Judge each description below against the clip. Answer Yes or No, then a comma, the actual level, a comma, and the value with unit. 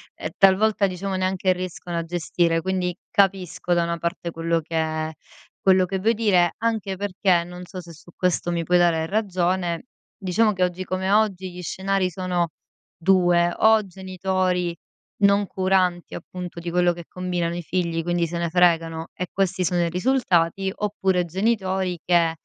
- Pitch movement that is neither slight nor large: No, narrow, 1.8 semitones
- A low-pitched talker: No, medium, 180 Hz